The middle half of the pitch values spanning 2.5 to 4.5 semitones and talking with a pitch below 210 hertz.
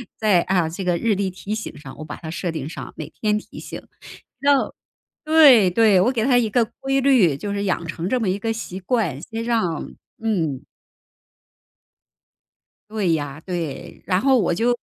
No: average, 5.1 semitones; high, 200 Hz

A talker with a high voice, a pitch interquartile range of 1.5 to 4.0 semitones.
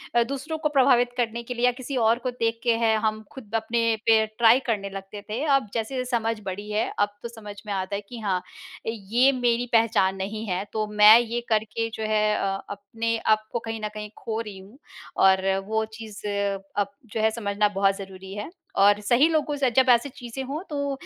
Yes: high, 225 Hz; average, 2.7 semitones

